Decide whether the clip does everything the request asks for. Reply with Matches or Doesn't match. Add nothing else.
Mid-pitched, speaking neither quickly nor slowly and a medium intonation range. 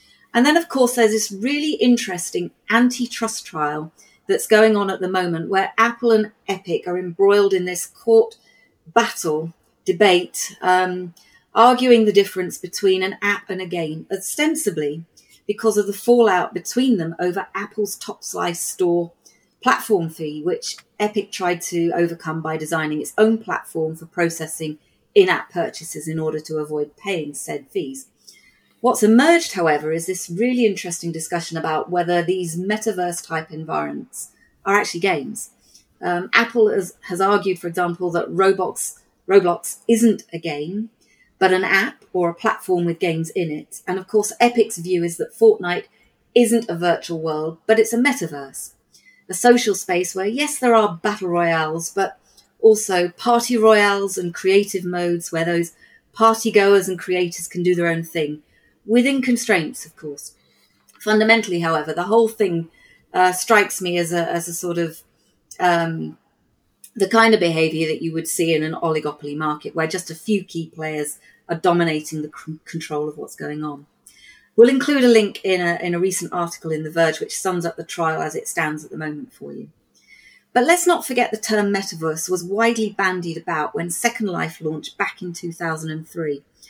Matches